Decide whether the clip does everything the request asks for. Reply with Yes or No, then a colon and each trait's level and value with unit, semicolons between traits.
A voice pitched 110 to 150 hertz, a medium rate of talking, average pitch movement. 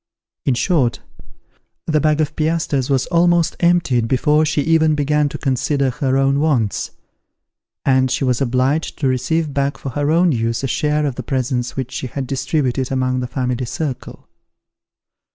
Yes: low, 135 Hz; average, 165 wpm; average, 3.1 semitones